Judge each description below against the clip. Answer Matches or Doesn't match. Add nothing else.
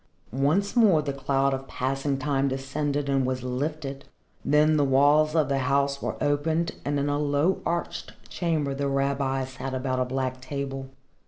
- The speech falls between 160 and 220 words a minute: Matches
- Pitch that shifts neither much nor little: Doesn't match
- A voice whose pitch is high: Doesn't match